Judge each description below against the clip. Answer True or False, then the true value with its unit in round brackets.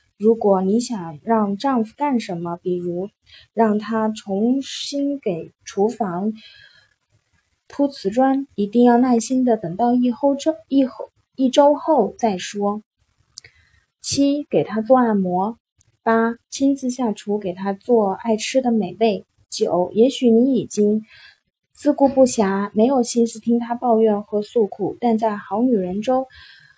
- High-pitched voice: True (230 Hz)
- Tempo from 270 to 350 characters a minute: False (195 characters per minute)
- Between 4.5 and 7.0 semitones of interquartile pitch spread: False (3.9 semitones)